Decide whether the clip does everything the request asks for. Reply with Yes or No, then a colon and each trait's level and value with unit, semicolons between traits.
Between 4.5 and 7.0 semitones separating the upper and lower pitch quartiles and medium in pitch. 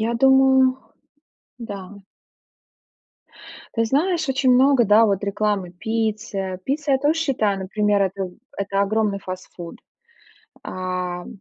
No: average, 5.2 semitones; high, 215 Hz